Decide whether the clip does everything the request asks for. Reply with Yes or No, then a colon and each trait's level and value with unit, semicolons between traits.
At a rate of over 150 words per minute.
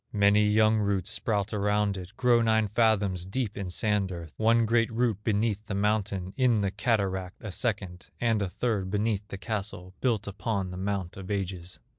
Yes: average, 180 wpm